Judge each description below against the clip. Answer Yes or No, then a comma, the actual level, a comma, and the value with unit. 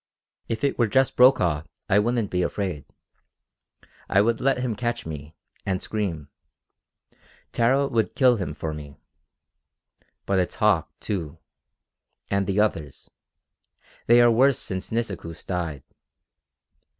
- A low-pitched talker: Yes, low, 100 Hz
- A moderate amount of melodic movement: No, wide, 6.0 semitones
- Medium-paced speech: No, slow, 125 wpm